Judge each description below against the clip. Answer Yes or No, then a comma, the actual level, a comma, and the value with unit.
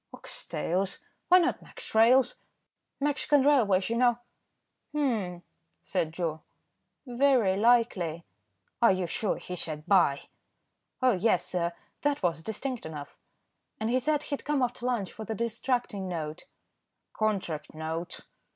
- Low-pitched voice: No, high, 215 Hz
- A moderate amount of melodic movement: No, wide, 6.3 semitones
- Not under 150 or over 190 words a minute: No, slow, 135 wpm